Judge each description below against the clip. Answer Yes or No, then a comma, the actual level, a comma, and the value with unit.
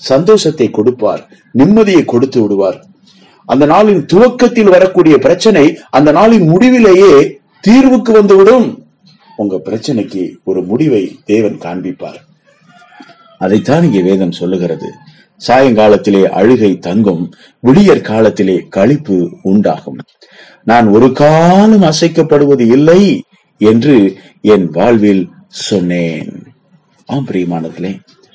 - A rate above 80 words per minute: Yes, average, 90 wpm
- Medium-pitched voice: Yes, medium, 145 Hz